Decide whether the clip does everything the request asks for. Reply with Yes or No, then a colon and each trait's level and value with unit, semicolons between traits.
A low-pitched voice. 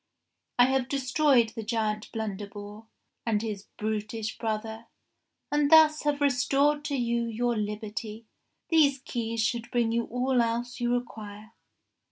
No: high, 235 Hz